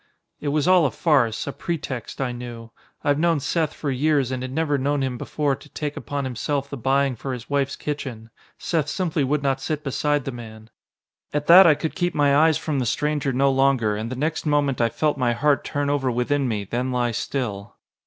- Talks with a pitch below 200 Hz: Yes, medium, 140 Hz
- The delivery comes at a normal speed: No, fast, 215 wpm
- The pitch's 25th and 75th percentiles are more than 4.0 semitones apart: No, average, 3.0 semitones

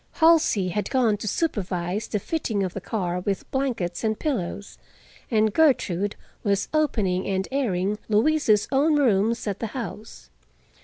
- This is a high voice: Yes, high, 210 Hz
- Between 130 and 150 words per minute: Yes, average, 145 wpm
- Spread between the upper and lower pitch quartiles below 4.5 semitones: No, wide, 5.5 semitones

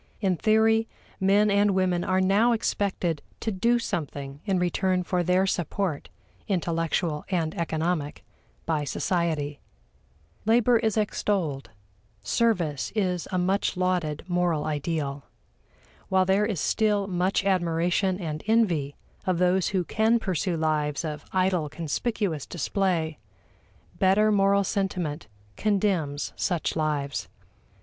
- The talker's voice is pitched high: No, medium, 180 Hz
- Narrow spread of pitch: No, average, 3.9 semitones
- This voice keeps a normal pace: No, slow, 120 wpm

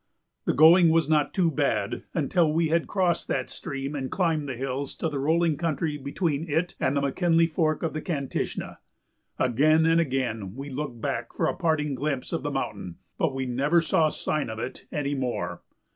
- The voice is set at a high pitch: No, medium, 150 Hz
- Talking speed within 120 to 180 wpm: No, average, 190 wpm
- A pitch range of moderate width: Yes, average, 3.3 semitones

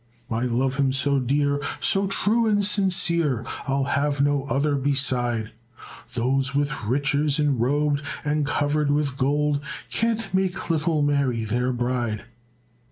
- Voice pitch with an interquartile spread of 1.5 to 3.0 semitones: Yes, narrow, 2.6 semitones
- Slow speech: Yes, slow, 130 wpm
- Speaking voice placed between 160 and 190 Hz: No, medium, 140 Hz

